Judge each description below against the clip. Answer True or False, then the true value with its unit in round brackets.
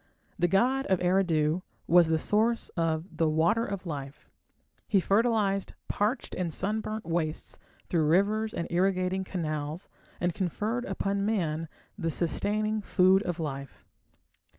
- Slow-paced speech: True (130 wpm)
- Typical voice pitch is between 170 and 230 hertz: True (185 Hz)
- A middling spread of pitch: True (4.1 semitones)